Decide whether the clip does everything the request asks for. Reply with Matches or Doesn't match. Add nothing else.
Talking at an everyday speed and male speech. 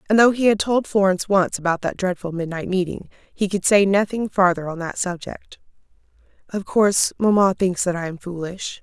Doesn't match